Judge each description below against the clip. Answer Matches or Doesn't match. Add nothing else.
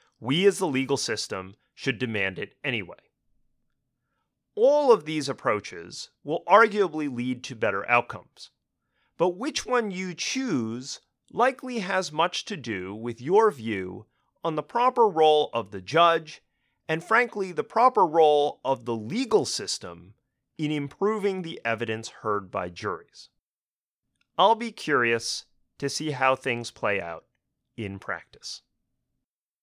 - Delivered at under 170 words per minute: Matches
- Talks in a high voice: Doesn't match